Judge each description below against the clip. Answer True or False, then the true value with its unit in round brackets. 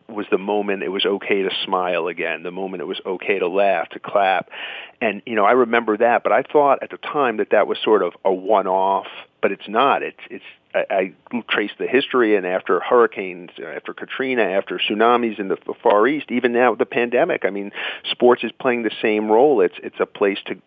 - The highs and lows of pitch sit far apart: False (3.5 semitones)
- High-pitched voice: False (110 Hz)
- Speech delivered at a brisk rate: True (220 wpm)